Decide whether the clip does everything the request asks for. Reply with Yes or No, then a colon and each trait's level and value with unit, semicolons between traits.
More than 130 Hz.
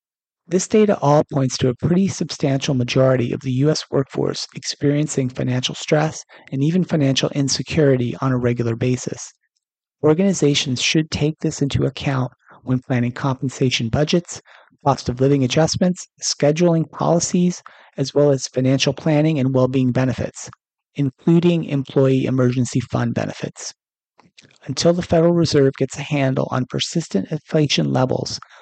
Yes: medium, 140 Hz